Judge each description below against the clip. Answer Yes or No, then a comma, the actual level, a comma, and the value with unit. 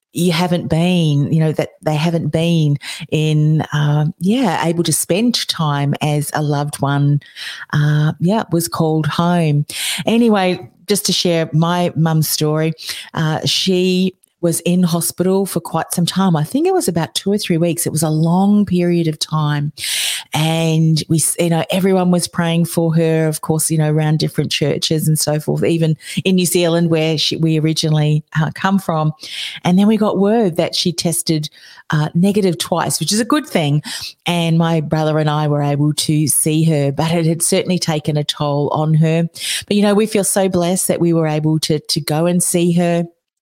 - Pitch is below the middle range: No, medium, 165 Hz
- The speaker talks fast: No, average, 190 wpm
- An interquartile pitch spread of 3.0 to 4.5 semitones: No, narrow, 2.5 semitones